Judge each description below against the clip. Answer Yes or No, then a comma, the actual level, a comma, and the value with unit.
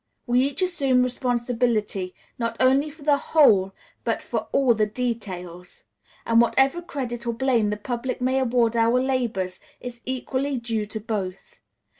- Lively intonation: No, average, 3.1 semitones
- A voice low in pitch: No, high, 240 Hz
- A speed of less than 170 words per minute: Yes, average, 150 wpm